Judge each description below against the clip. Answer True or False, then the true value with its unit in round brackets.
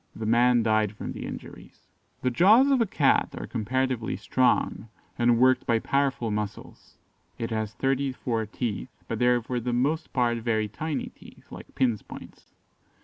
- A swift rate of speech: False (170 wpm)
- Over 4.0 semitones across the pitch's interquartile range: False (2.9 semitones)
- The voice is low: True (120 Hz)